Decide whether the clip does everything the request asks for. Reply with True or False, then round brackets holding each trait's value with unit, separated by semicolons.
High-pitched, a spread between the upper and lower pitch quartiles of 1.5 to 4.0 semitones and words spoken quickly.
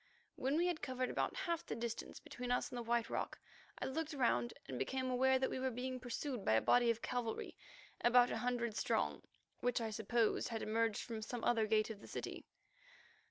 True (245 Hz; 2.4 semitones; 210 wpm)